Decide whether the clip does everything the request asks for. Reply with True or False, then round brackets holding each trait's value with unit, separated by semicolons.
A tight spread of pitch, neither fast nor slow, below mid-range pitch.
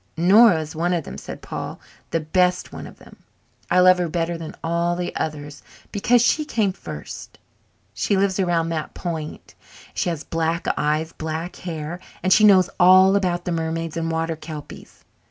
False (2.3 semitones; 185 wpm; 170 Hz)